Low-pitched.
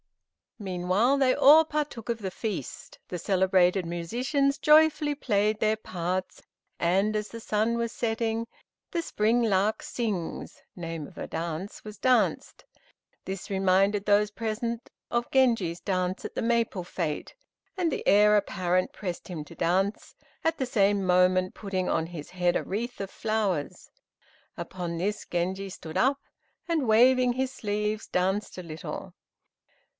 No: high, 205 Hz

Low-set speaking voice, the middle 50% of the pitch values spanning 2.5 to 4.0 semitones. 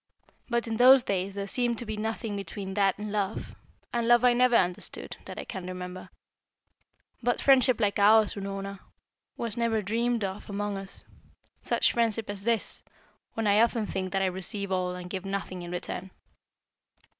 No: high, 205 Hz; average, 3.2 semitones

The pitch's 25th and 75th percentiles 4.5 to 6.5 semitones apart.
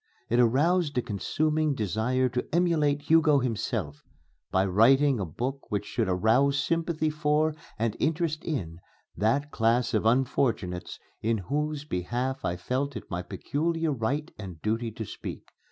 Yes: wide, 5.6 semitones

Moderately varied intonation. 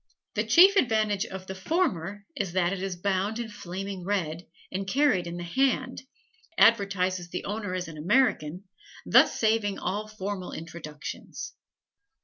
Yes: average, 3.2 semitones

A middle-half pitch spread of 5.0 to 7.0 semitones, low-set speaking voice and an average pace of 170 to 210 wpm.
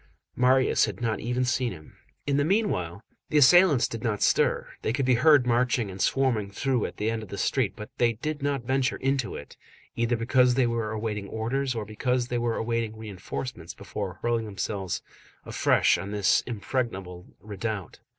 No: average, 3.6 semitones; low, 115 Hz; average, 180 wpm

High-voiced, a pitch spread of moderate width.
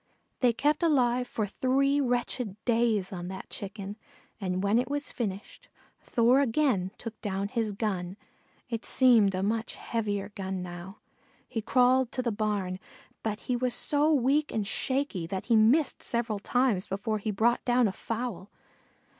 Yes: high, 225 Hz; average, 4.1 semitones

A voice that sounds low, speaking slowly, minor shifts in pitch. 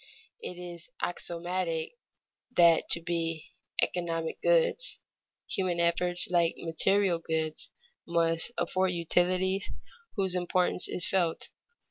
No: medium, 175 Hz; slow, 105 wpm; narrow, 1.7 semitones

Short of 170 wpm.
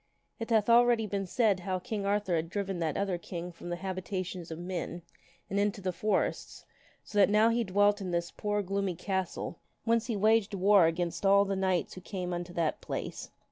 No: average, 200 wpm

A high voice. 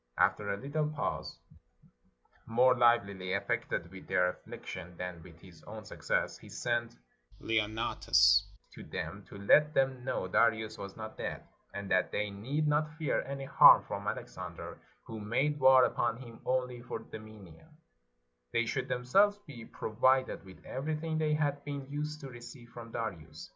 No: low, 120 Hz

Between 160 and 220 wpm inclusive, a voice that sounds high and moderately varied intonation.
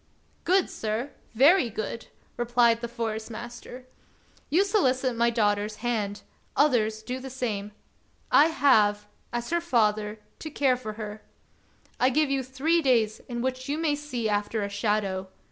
No: average, 150 wpm; high, 240 Hz; average, 3.8 semitones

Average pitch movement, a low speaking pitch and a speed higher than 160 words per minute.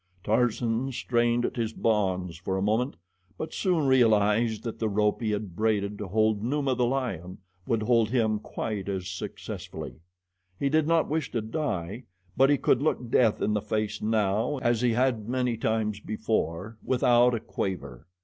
Yes: average, 3.1 semitones; low, 110 Hz; average, 170 wpm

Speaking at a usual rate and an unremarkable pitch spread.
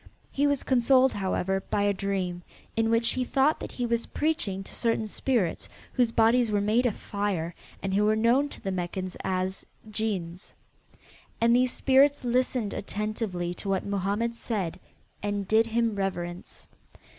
Yes: average, 160 wpm; average, 3.7 semitones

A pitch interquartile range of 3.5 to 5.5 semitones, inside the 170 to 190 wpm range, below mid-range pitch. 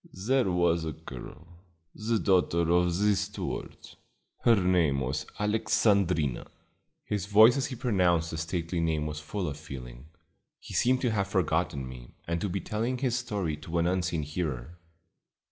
No: average, 5.0 semitones; average, 160 wpm; very low, 85 Hz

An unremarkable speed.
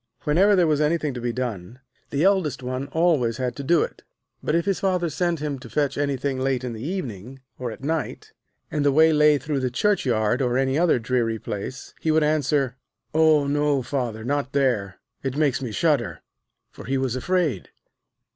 Yes: average, 195 wpm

